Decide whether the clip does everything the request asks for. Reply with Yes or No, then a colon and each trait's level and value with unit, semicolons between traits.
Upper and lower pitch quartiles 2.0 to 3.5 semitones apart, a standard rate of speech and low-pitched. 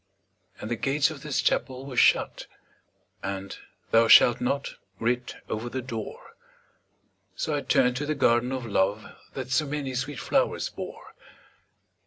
Yes: average, 2.9 semitones; average, 150 wpm; low, 125 Hz